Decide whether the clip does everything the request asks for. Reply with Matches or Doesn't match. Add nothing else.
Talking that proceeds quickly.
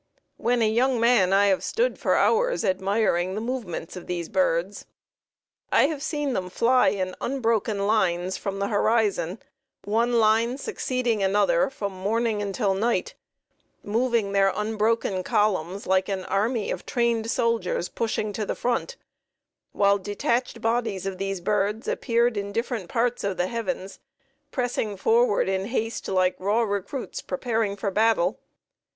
Doesn't match